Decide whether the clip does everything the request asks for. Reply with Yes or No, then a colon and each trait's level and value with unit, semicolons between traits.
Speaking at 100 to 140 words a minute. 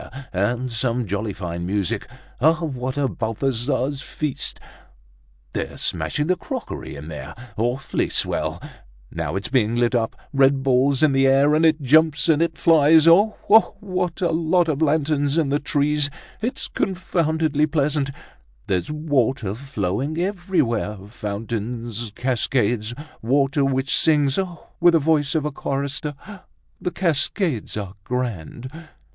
Yes: slow, 135 wpm